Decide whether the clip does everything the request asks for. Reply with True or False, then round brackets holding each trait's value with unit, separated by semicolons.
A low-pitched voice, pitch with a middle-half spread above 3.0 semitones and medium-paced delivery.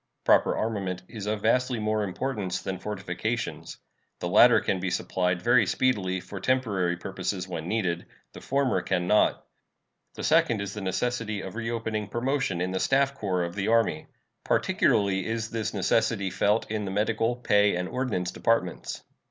True (105 Hz; 3.7 semitones; 160 wpm)